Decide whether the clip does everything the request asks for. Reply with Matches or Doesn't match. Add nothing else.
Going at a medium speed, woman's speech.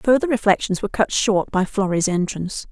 Matches